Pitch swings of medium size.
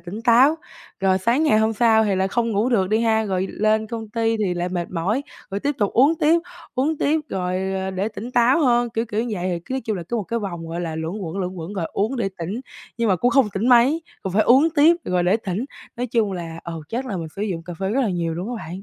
Yes: average, 4.5 semitones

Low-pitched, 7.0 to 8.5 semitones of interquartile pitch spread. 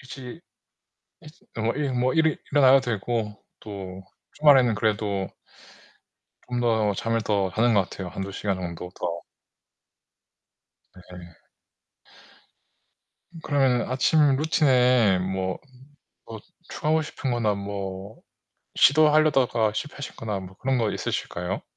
No: low, 115 Hz; wide, 5.4 semitones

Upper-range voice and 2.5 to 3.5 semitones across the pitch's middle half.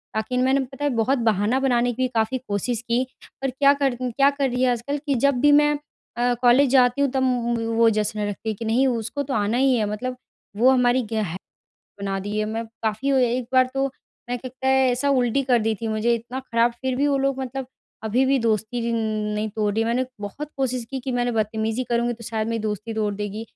Yes: high, 245 Hz; average, 3.1 semitones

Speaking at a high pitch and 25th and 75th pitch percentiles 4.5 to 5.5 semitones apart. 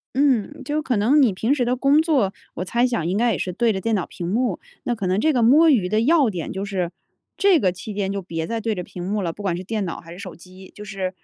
Yes: high, 210 Hz; average, 5.2 semitones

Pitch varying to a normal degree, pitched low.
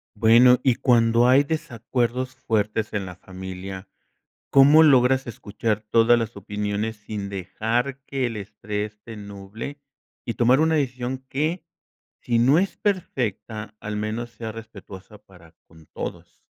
Yes: average, 3.7 semitones; low, 115 Hz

